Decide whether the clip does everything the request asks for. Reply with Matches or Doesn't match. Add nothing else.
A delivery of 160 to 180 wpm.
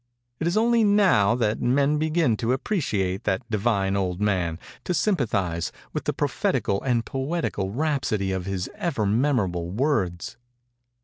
Doesn't match